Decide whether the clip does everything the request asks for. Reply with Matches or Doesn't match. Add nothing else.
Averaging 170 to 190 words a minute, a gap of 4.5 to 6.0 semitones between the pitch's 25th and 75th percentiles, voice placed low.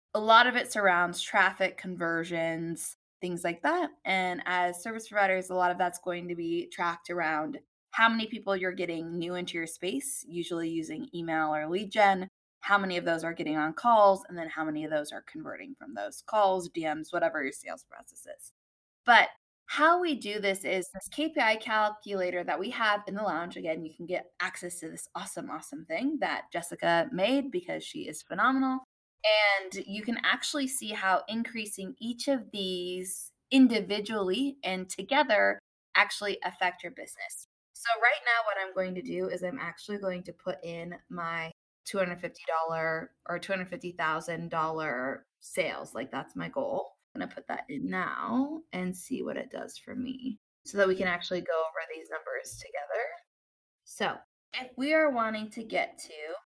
Doesn't match